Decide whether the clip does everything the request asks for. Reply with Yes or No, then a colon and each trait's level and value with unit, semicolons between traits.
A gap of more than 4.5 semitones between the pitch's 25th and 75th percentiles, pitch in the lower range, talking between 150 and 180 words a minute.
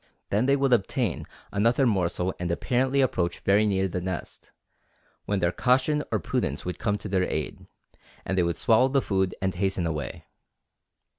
Yes: wide, 5.4 semitones; low, 100 Hz; average, 170 wpm